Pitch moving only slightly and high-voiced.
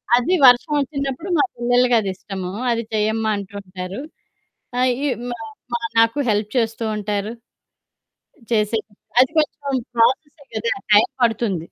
No: average, 3.2 semitones; high, 230 Hz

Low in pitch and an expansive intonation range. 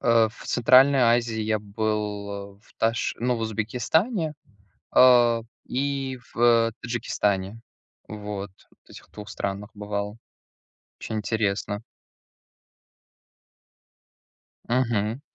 No: low, 110 Hz; average, 2.8 semitones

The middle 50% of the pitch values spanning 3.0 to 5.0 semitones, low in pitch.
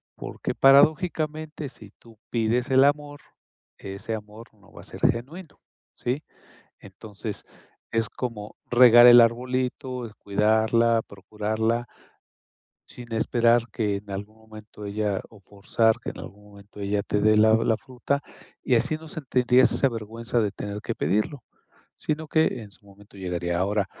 Yes: average, 3.4 semitones; low, 115 Hz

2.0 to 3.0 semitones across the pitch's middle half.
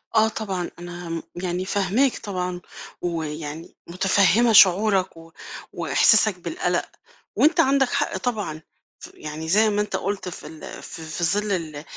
No: average, 4.3 semitones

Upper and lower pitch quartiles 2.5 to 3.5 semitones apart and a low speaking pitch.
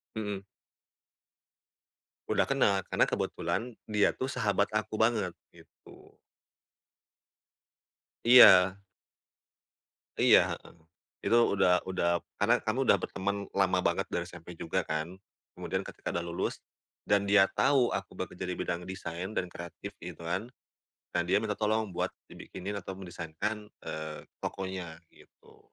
Yes: average, 3.2 semitones; very low, 95 Hz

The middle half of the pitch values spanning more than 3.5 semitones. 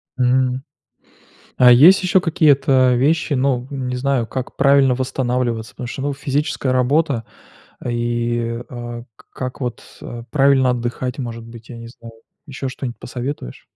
No: narrow, 2.5 semitones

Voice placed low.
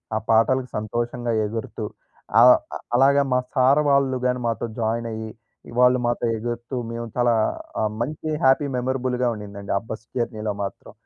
Yes: low, 120 Hz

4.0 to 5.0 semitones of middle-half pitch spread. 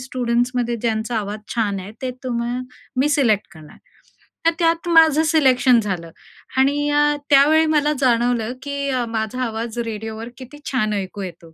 Yes: average, 4.3 semitones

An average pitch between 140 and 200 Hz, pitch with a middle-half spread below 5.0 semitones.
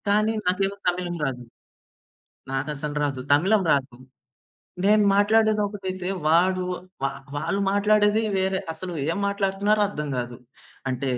No: high, 190 Hz; wide, 5.4 semitones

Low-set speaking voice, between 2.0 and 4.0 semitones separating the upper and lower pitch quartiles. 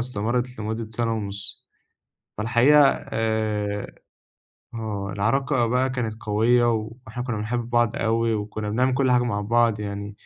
Yes: low, 115 Hz; narrow, 2.5 semitones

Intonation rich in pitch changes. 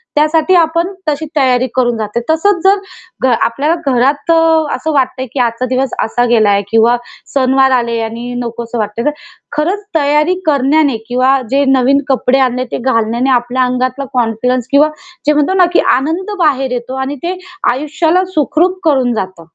No: average, 3.7 semitones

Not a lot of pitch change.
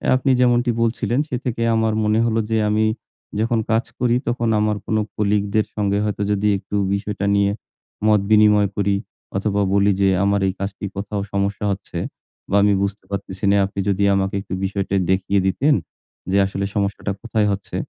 Yes: narrow, 1.7 semitones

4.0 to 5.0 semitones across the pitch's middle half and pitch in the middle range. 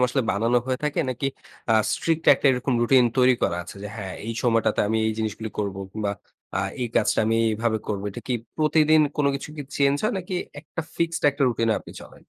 No: average, 4.3 semitones; low, 120 Hz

